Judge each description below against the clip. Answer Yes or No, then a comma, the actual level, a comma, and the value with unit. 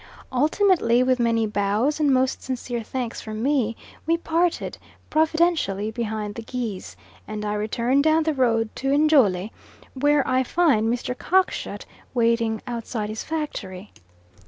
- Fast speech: No, slow, 135 wpm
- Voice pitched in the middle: No, high, 245 Hz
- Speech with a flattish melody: No, average, 5.2 semitones